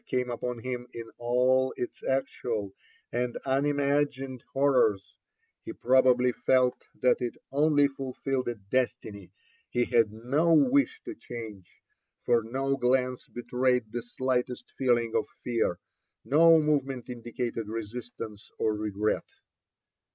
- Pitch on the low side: Yes, low, 125 Hz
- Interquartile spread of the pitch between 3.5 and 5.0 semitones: No, narrow, 2.5 semitones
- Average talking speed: No, slow, 120 wpm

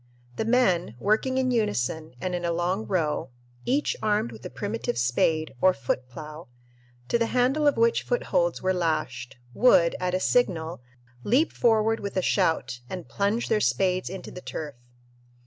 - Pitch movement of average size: No, wide, 6.3 semitones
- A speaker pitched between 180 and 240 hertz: Yes, medium, 185 Hz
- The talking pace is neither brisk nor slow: Yes, average, 165 wpm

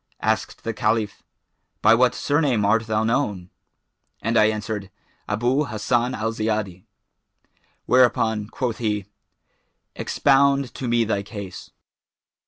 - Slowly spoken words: Yes, slow, 115 wpm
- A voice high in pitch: No, low, 110 Hz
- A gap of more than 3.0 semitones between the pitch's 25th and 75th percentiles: No, average, 2.7 semitones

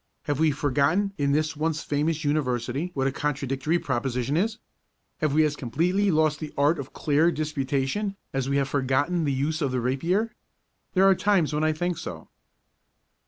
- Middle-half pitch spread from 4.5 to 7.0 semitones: No, average, 3.3 semitones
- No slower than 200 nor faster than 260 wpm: No, average, 175 wpm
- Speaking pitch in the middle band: Yes, medium, 150 Hz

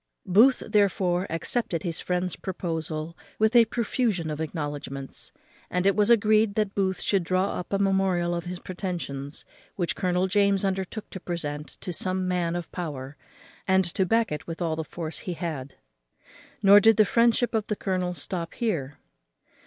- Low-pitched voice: No, medium, 185 Hz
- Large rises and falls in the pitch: No, average, 3.2 semitones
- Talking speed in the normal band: Yes, average, 170 wpm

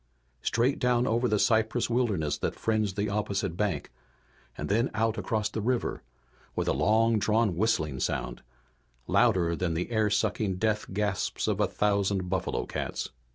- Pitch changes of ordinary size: Yes, average, 3.1 semitones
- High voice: No, low, 105 Hz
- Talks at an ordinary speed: Yes, average, 155 wpm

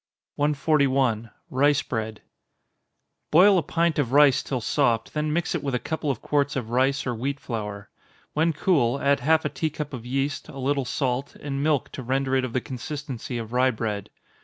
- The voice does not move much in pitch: No, average, 3.0 semitones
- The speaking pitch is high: No, low, 135 Hz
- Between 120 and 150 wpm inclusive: No, average, 190 wpm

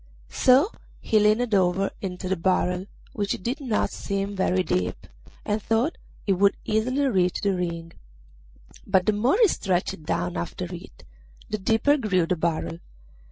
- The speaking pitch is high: Yes, high, 195 Hz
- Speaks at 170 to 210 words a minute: No, average, 155 wpm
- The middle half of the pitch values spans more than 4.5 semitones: No, average, 3.6 semitones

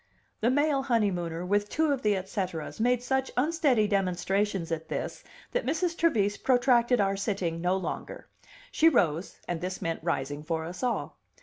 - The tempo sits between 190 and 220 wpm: No, average, 170 wpm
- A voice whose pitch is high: Yes, high, 205 Hz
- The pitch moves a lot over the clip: Yes, wide, 6.3 semitones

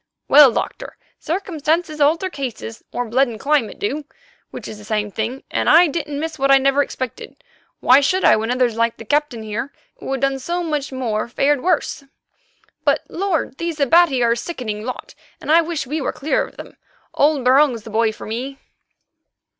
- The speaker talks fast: No, average, 190 wpm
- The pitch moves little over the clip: No, average, 4.6 semitones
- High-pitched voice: Yes, very high, 275 Hz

